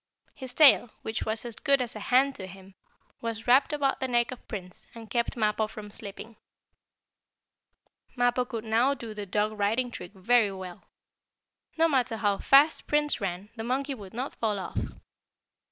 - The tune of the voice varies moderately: Yes, average, 3.6 semitones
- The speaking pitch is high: Yes, high, 230 Hz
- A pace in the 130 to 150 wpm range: No, average, 170 wpm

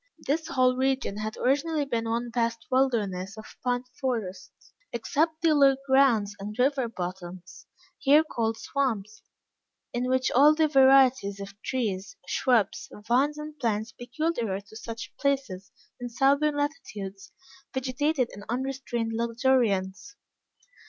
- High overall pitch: Yes, high, 245 Hz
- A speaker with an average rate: No, slow, 125 wpm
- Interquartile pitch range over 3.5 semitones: Yes, average, 4.2 semitones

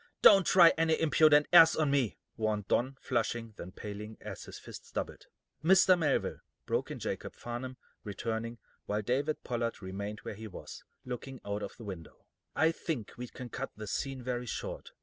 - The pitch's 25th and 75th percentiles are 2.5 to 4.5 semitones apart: No, wide, 5.6 semitones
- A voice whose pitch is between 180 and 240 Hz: No, low, 120 Hz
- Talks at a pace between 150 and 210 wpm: Yes, average, 175 wpm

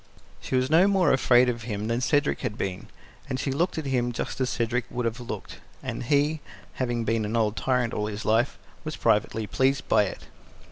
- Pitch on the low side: Yes, low, 125 Hz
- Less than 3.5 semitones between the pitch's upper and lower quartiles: Yes, average, 3.1 semitones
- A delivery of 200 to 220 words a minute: Yes, fast, 205 wpm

